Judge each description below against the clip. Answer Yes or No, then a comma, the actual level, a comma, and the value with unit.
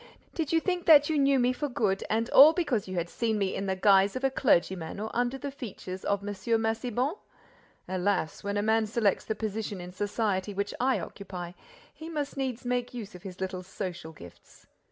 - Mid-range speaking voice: No, high, 215 Hz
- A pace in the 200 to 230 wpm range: Yes, fast, 205 wpm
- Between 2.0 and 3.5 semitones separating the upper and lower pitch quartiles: No, average, 5.2 semitones